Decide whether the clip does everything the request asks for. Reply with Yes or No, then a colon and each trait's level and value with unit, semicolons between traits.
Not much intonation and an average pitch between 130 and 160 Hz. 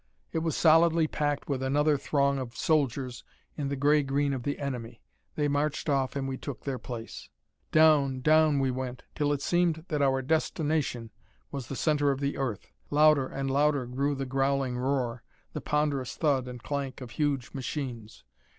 Yes: narrow, 2.3 semitones; medium, 140 Hz